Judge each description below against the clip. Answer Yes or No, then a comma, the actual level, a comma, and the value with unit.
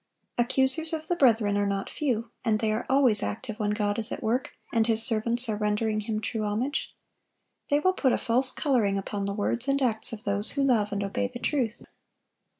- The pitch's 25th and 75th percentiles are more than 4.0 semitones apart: No, average, 3.7 semitones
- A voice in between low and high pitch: No, high, 225 Hz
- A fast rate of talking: Yes, fast, 210 wpm